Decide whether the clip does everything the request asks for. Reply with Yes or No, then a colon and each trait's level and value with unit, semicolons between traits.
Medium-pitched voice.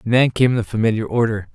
No: low, 115 Hz